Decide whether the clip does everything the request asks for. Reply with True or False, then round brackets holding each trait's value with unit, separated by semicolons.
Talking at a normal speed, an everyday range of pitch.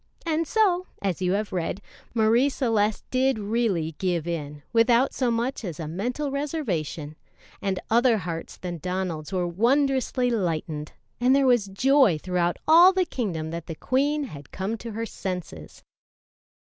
False (155 wpm; 7.1 semitones)